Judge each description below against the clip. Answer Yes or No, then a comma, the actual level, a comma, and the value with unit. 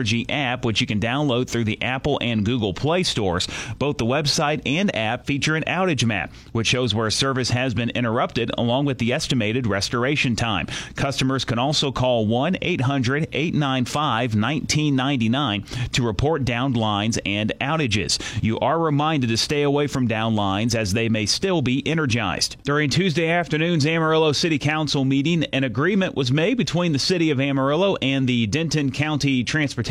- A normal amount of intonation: Yes, average, 4.5 semitones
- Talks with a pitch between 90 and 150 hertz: Yes, low, 135 Hz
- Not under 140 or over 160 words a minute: No, average, 175 wpm